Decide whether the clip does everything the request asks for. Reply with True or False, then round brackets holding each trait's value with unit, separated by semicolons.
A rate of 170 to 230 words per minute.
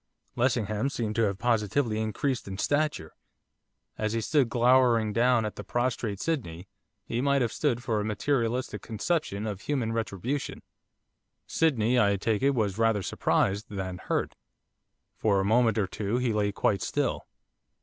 False (155 wpm)